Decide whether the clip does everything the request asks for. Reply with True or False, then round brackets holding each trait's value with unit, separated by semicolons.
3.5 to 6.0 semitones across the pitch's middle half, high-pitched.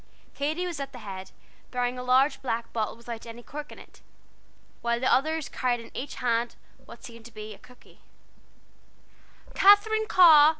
True (4.3 semitones; 250 Hz)